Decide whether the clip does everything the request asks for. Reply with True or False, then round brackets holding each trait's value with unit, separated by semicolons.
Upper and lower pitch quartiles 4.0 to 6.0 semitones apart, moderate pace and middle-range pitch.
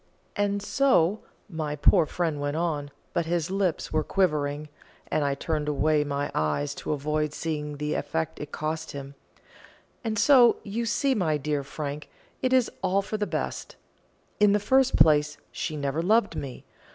True (5.2 semitones; 165 wpm; 155 Hz)